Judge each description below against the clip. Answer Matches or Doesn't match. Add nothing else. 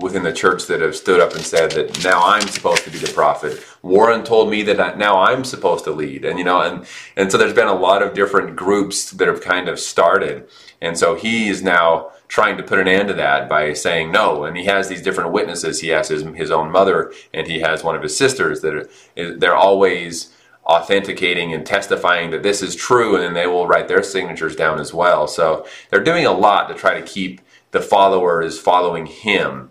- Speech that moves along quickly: Matches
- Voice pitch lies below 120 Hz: Matches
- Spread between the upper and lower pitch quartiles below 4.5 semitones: Doesn't match